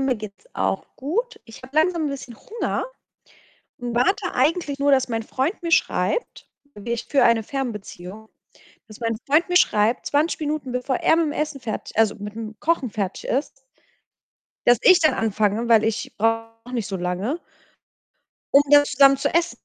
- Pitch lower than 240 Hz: No, very high, 250 Hz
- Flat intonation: No, average, 5.1 semitones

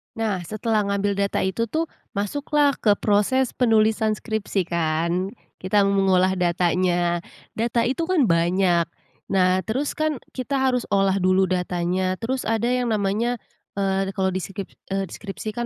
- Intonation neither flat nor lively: Yes, average, 3.7 semitones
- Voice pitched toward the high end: Yes, high, 200 Hz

